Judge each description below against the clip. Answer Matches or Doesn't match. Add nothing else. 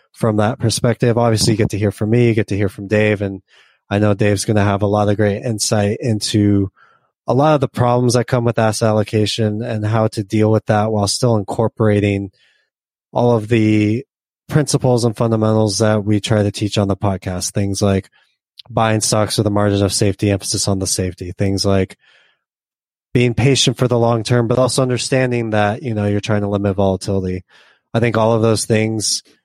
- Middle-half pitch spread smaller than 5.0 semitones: Matches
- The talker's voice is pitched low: Matches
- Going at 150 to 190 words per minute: Doesn't match